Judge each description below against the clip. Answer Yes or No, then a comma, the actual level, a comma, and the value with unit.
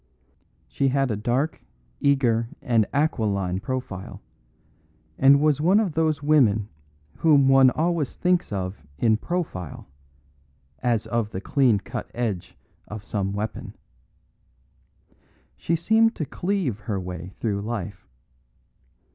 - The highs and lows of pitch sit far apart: Yes, wide, 6.7 semitones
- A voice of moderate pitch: No, low, 120 Hz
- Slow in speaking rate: Yes, slow, 120 wpm